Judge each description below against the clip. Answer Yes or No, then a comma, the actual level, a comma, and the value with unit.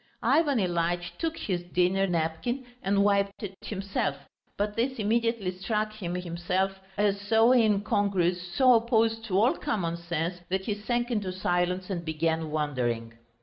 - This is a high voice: Yes, high, 195 Hz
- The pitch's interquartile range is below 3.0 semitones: No, average, 4.0 semitones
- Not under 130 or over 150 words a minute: Yes, average, 145 wpm